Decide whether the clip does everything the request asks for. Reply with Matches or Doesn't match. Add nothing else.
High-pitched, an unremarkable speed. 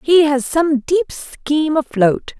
Matches